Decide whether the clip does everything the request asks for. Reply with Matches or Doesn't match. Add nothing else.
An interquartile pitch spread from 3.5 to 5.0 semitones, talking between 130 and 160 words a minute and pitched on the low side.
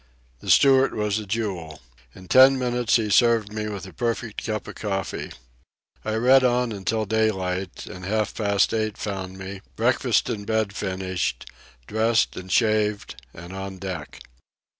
Doesn't match